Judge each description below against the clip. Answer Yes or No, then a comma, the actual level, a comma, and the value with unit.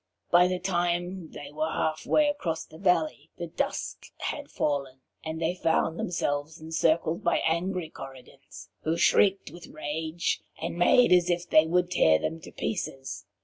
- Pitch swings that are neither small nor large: No, narrow, 2.2 semitones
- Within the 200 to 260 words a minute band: No, average, 160 wpm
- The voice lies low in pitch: No, medium, 165 Hz